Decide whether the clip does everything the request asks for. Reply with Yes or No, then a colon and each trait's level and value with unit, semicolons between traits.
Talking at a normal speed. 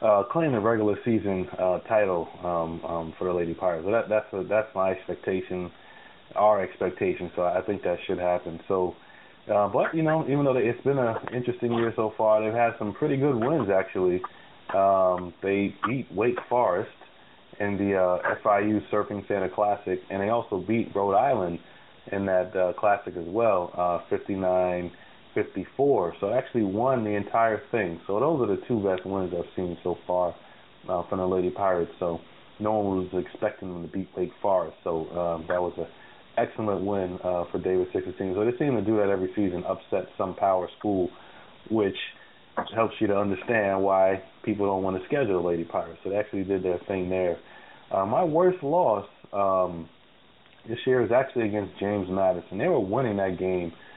Yes: average, 190 wpm